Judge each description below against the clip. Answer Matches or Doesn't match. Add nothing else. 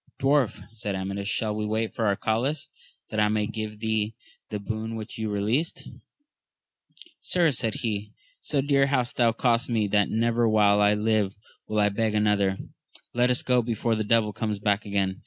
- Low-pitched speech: Matches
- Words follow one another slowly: Doesn't match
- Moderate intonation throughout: Doesn't match